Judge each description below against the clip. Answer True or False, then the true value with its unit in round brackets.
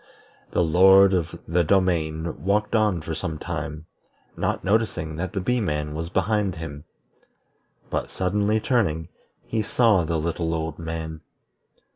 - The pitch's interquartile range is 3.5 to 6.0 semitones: True (3.8 semitones)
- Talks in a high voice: False (85 Hz)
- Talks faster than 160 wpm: False (140 wpm)